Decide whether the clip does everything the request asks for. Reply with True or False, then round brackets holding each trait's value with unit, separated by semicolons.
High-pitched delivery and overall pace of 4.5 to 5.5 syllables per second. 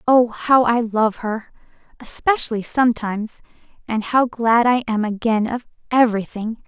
True (230 Hz; 4.7 syllables/s)